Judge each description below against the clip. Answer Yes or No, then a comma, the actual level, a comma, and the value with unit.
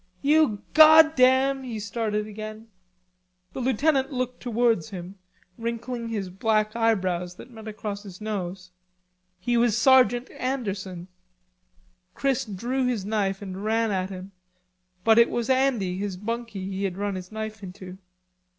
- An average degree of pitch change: Yes, average, 3.9 semitones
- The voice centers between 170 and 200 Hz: No, high, 220 Hz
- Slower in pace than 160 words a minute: Yes, average, 140 wpm